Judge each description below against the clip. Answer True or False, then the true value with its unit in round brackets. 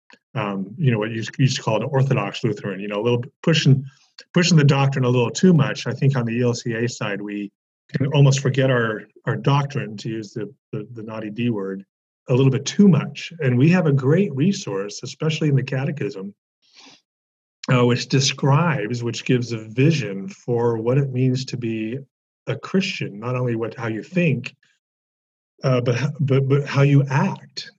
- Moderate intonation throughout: True (3.7 semitones)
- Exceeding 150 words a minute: True (190 wpm)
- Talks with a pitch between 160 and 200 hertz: False (130 Hz)